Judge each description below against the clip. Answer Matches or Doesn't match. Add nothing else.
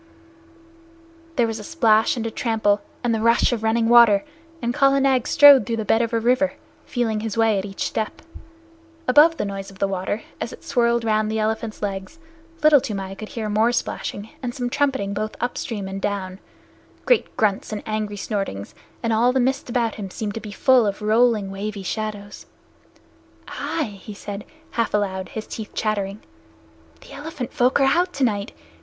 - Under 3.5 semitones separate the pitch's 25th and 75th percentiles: Matches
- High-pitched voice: Matches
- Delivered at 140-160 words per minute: Doesn't match